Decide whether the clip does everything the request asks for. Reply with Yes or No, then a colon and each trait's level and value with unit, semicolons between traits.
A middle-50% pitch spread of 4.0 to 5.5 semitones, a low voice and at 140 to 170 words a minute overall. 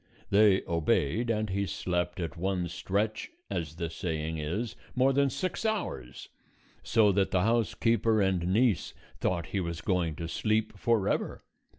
Yes: average, 4.7 semitones; very low, 95 Hz; average, 150 wpm